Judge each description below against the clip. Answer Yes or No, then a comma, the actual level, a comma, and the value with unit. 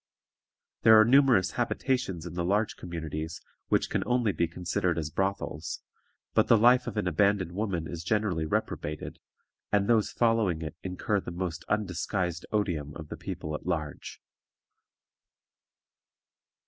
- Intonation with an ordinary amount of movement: Yes, average, 4.6 semitones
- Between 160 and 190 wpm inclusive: No, average, 140 wpm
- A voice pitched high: No, very low, 90 Hz